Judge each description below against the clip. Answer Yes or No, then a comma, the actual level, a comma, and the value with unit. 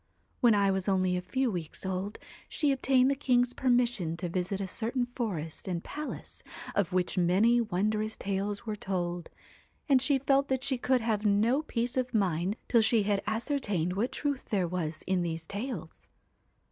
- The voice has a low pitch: No, high, 210 Hz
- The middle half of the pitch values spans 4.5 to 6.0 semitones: Yes, average, 5.2 semitones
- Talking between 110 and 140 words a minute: No, average, 180 wpm